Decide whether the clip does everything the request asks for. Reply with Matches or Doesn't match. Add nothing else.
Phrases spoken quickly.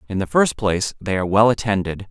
Matches